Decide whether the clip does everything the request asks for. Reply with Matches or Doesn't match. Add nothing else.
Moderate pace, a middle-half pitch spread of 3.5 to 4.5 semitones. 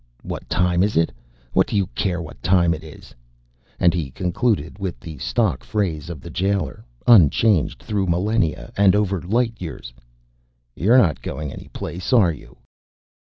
Matches